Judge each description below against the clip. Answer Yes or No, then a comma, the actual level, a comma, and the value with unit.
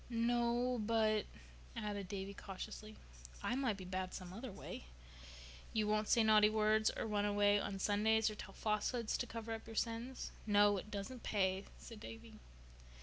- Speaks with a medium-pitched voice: No, high, 215 Hz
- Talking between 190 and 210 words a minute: No, average, 165 wpm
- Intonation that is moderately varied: No, narrow, 1.9 semitones